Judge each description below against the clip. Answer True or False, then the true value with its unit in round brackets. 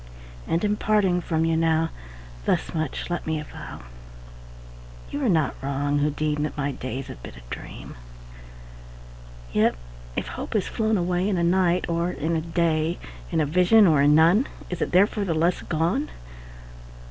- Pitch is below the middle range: False (165 Hz)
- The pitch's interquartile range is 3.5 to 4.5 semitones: False (3.1 semitones)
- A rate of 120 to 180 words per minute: True (170 wpm)